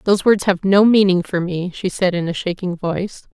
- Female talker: Yes, female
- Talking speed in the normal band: No, fast, 235 wpm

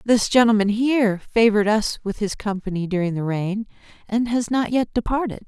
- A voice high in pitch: Yes, high, 215 Hz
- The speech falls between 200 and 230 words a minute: No, average, 155 wpm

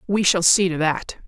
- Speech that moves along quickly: Yes, fast, 235 wpm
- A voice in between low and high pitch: Yes, medium, 180 Hz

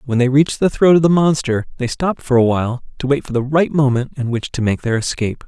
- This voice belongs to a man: Yes, male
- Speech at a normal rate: No, fast, 275 wpm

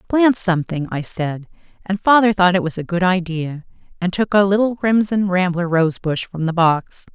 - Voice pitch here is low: No, medium, 180 Hz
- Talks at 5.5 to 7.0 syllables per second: No, 4.9 syllables/s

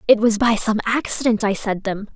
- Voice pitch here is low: No, high, 215 Hz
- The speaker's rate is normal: No, fast, 225 wpm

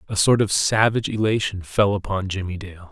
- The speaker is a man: Yes, male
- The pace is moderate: Yes, average, 185 wpm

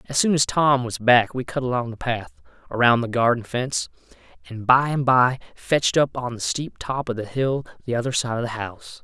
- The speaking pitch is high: No, low, 125 Hz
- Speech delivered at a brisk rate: Yes, fast, 225 wpm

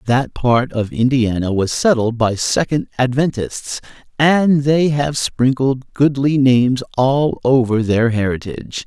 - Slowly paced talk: Yes, slow, 130 wpm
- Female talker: No, male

